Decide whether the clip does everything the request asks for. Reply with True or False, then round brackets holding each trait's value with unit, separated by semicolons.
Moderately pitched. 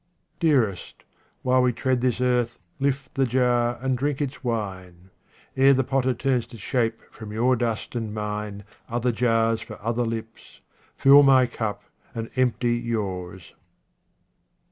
False (120 Hz)